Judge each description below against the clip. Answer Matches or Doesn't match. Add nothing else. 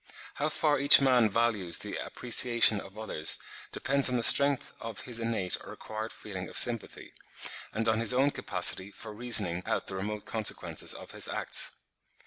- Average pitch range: Matches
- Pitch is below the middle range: Matches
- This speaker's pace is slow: Doesn't match